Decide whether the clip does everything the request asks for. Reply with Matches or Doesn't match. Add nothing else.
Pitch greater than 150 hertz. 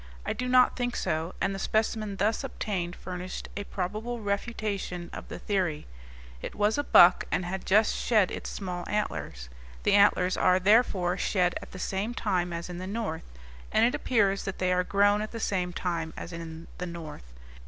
Matches